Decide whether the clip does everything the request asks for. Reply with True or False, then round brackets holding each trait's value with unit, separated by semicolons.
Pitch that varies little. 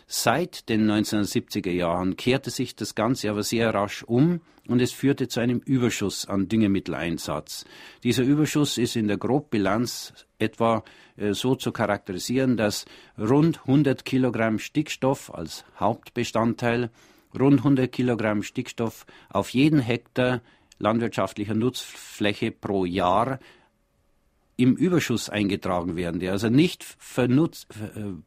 False (3.8 semitones)